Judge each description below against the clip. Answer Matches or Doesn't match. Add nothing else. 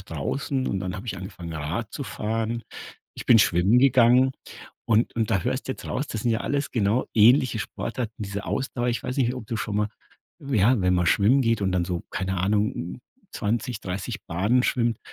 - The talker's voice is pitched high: Doesn't match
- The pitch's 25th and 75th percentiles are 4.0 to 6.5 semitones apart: Matches